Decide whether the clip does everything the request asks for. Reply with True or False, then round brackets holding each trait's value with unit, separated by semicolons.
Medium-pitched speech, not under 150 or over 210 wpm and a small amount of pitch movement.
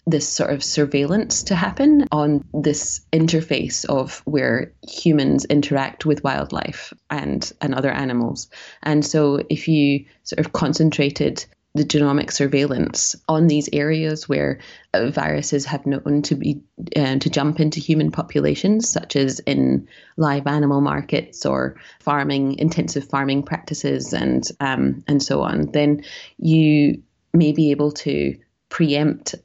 False (145 Hz; 140 wpm; 1.8 semitones)